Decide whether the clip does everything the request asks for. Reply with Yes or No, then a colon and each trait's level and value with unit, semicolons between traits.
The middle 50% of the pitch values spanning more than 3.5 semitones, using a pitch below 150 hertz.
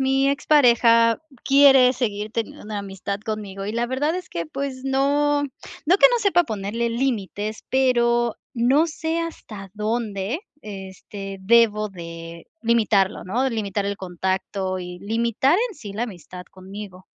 No: average, 5.1 semitones; high, 225 Hz